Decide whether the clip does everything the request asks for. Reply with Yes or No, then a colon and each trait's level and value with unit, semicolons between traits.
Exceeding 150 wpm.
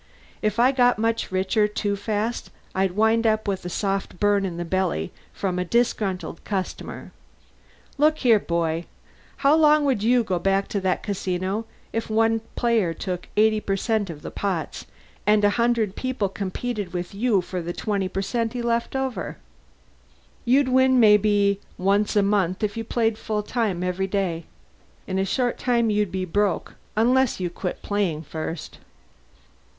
Yes: average, 160 wpm